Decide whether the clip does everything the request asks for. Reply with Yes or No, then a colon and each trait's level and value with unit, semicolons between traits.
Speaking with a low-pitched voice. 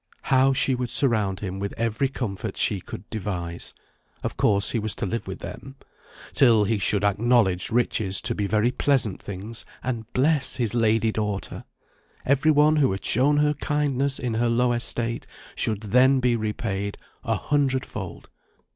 Yes: low, 115 Hz